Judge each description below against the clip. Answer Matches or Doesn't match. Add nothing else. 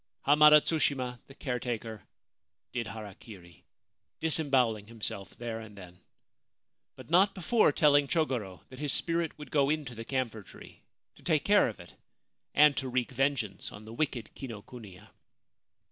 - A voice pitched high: Doesn't match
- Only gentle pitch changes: Doesn't match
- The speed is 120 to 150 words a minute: Matches